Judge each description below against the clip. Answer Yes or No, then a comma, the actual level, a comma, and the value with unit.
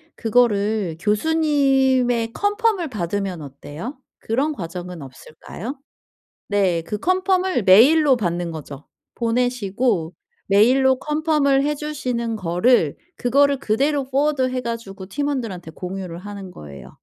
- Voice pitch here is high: Yes, high, 230 Hz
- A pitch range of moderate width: No, wide, 7.0 semitones